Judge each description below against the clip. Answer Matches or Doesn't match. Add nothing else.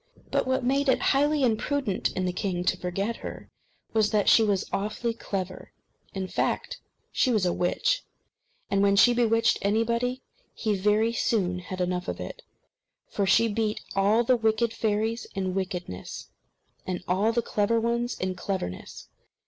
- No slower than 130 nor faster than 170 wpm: Matches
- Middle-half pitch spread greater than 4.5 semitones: Doesn't match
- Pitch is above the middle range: Matches